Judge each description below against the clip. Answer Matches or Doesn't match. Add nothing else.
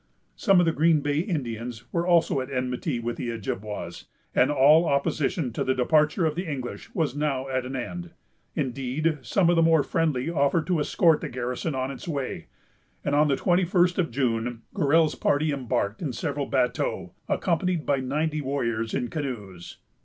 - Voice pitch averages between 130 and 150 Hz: Matches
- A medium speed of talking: Matches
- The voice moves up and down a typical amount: Matches